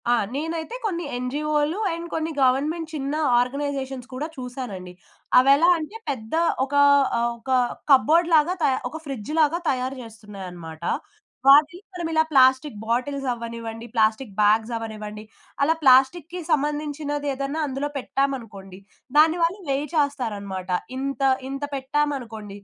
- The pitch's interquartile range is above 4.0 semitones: Yes, average, 4.5 semitones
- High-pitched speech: Yes, very high, 275 Hz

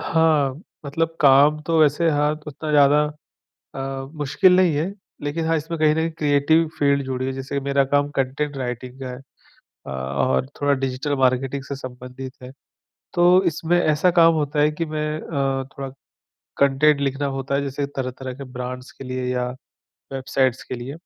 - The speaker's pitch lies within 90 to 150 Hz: Yes, medium, 140 Hz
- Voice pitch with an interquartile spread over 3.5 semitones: No, narrow, 2.6 semitones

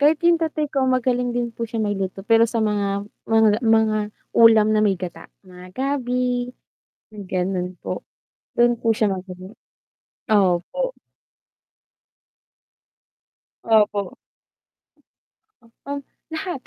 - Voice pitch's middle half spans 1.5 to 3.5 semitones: No, average, 3.9 semitones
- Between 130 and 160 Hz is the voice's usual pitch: No, high, 225 Hz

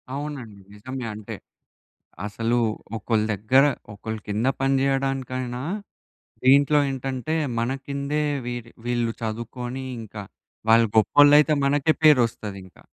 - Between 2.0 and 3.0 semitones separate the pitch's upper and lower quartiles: No, average, 3.5 semitones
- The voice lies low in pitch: Yes, low, 125 Hz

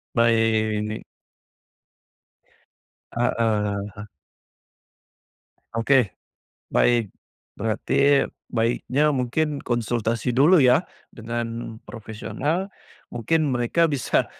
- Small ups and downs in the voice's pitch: No, average, 3.6 semitones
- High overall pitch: No, low, 120 Hz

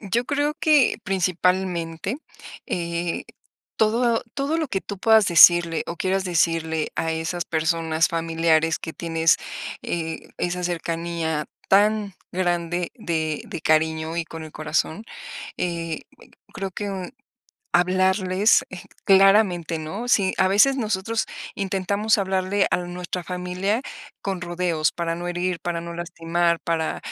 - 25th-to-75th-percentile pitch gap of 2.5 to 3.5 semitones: Yes, average, 2.8 semitones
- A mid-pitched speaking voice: Yes, medium, 175 Hz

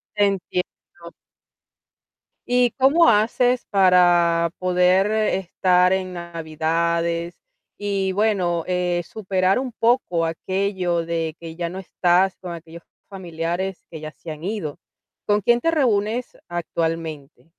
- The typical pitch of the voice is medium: Yes, medium, 180 Hz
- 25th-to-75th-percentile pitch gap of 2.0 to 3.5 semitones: Yes, average, 2.9 semitones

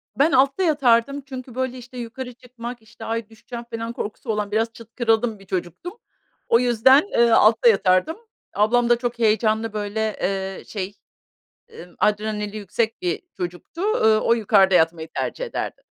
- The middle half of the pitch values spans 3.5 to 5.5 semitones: No, average, 3.0 semitones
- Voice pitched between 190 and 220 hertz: No, high, 230 Hz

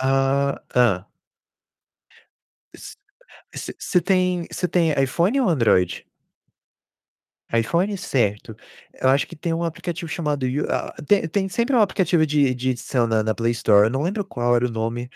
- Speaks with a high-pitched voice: No, medium, 140 Hz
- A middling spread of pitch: No, wide, 6.6 semitones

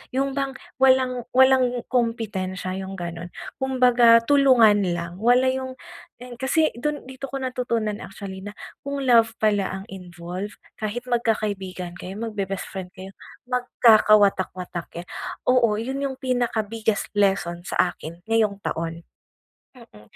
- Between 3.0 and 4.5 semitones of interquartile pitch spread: No, average, 4.9 semitones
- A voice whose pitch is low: No, high, 220 Hz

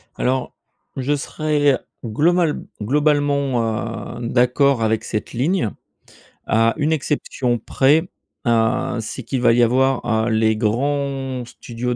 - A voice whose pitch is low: Yes, low, 125 Hz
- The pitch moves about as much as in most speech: Yes, average, 3.7 semitones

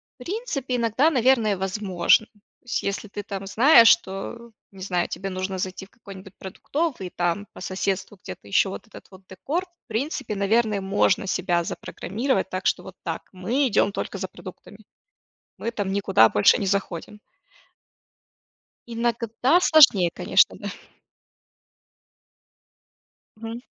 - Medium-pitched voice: No, high, 200 Hz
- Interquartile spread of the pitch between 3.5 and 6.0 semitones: Yes, average, 3.8 semitones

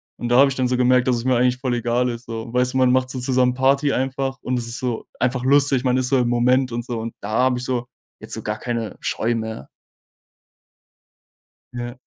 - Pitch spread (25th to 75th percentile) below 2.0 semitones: Yes, narrow, 1.4 semitones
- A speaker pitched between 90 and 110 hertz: No, low, 125 Hz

